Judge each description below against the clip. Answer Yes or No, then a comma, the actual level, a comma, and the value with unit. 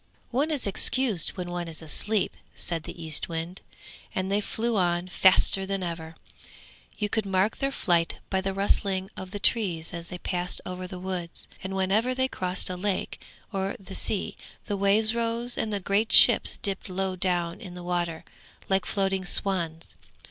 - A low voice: No, high, 190 Hz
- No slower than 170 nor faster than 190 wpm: Yes, average, 175 wpm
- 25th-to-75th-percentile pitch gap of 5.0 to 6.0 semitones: No, narrow, 2.5 semitones